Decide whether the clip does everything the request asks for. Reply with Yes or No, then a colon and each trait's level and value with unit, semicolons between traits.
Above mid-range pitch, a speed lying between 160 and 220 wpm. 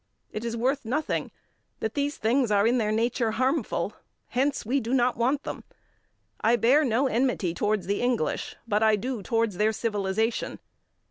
Yes: high, 230 Hz; average, 165 wpm